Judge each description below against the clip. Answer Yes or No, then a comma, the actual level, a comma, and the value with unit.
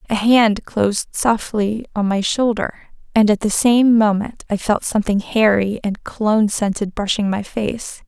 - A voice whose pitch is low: No, high, 215 Hz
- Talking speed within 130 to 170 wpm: Yes, average, 165 wpm